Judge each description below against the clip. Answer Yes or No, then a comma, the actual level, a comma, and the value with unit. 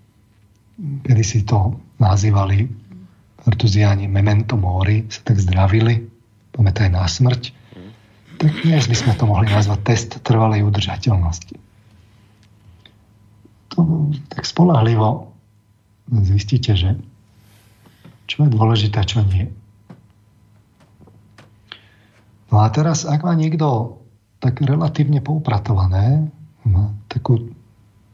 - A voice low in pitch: Yes, low, 110 Hz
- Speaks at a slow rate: Yes, slow, 95 wpm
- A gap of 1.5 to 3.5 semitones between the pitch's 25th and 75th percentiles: Yes, average, 2.9 semitones